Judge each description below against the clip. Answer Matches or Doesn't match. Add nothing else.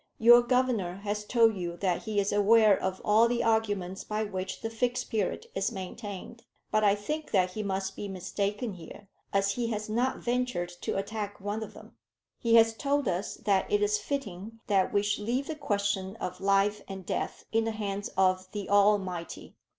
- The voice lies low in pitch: Doesn't match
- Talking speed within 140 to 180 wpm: Doesn't match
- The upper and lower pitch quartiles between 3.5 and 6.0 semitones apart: Doesn't match